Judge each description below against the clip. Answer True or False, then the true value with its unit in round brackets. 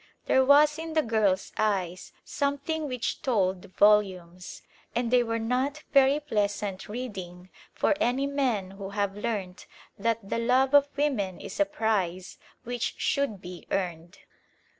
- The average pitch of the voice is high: True (225 Hz)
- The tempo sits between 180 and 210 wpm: False (140 wpm)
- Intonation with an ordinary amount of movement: False (5.9 semitones)